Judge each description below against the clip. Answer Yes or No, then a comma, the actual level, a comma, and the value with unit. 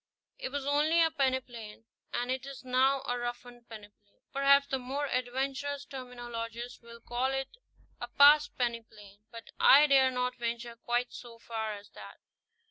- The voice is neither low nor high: No, very high, 250 Hz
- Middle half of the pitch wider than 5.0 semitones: No, average, 2.8 semitones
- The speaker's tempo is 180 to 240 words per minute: No, average, 160 wpm